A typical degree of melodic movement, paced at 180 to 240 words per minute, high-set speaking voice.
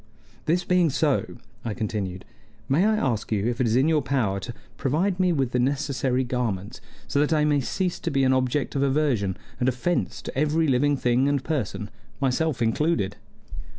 No: average, 4.1 semitones; average, 185 wpm; low, 135 Hz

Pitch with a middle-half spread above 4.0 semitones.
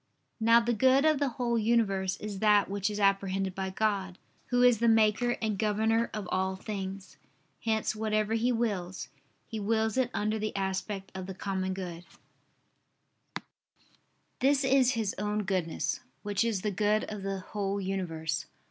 No: average, 2.8 semitones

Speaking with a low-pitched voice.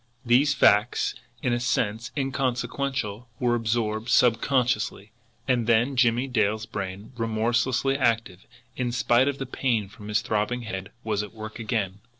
Yes: low, 115 Hz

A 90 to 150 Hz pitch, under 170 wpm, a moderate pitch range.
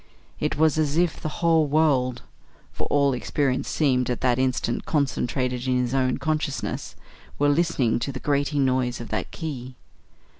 Yes: low, 135 Hz; average, 160 wpm; average, 3.1 semitones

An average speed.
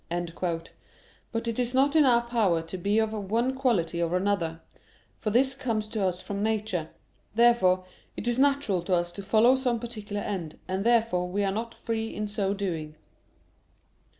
Yes: average, 175 wpm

